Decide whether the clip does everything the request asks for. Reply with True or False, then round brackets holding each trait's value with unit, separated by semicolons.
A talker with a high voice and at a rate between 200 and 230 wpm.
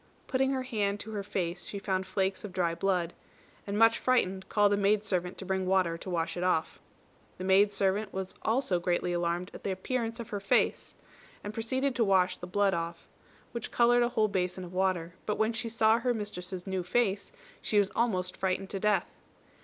True (195 Hz; 205 wpm)